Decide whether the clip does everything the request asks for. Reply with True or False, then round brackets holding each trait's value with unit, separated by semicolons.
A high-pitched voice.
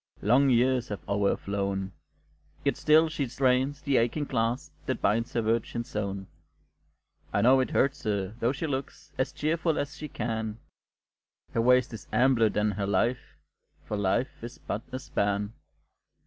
False (120 Hz)